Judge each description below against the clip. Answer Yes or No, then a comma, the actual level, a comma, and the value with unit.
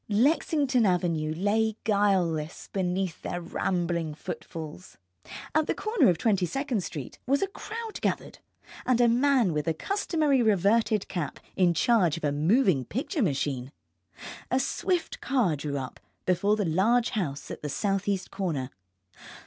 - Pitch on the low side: No, high, 195 Hz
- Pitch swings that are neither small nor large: No, wide, 7.0 semitones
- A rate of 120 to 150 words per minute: Yes, average, 145 wpm